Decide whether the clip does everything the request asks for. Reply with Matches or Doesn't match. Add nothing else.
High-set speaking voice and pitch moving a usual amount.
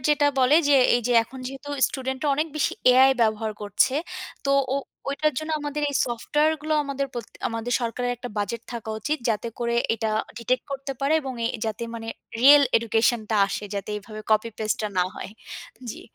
Matches